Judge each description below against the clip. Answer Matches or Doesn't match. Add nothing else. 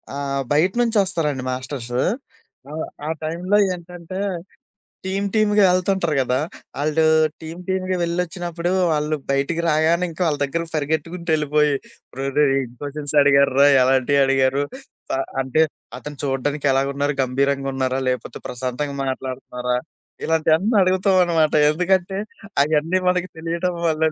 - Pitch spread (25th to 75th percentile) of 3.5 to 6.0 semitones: Matches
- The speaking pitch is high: Doesn't match